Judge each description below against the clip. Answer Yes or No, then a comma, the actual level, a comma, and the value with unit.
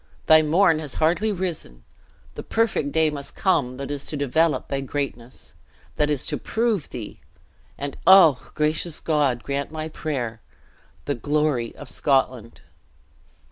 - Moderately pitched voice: Yes, medium, 150 Hz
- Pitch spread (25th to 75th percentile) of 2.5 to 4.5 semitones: Yes, average, 3.2 semitones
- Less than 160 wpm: Yes, average, 140 wpm